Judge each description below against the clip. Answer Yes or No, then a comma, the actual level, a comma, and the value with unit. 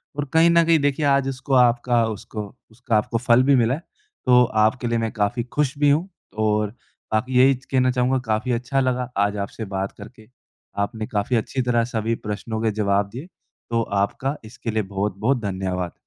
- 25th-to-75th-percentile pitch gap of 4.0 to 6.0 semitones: No, average, 3.4 semitones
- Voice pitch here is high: No, low, 120 Hz